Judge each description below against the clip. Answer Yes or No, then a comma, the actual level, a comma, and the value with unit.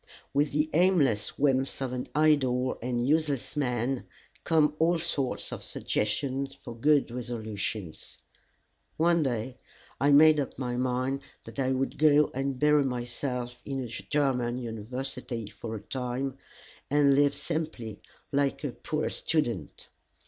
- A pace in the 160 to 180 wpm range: No, slow, 135 wpm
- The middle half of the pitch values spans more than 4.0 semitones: No, average, 3.2 semitones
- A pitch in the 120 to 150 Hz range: Yes, low, 135 Hz